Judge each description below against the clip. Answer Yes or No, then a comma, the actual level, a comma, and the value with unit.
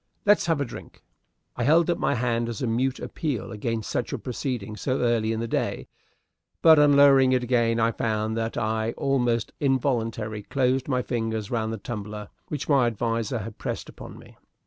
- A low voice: Yes, low, 120 Hz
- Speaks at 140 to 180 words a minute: No, average, 190 wpm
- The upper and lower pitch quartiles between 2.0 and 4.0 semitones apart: Yes, average, 2.9 semitones